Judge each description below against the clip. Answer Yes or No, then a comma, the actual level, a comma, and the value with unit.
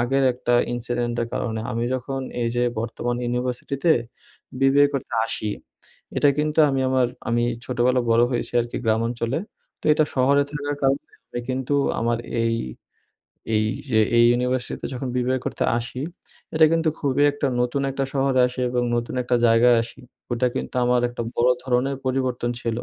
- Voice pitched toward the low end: Yes, low, 125 Hz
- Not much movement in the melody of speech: Yes, narrow, 2.2 semitones